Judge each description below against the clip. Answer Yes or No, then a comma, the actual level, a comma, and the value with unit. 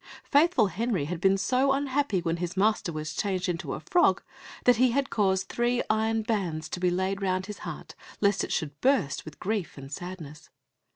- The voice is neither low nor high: No, high, 195 Hz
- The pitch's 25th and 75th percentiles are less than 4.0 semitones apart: No, average, 5.0 semitones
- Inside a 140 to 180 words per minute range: No, average, 190 wpm